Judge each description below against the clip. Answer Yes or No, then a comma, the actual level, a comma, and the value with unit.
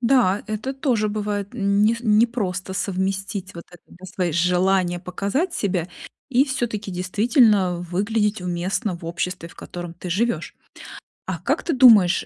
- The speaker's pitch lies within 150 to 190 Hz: No, high, 200 Hz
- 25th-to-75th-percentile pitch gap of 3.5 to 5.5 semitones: Yes, average, 3.8 semitones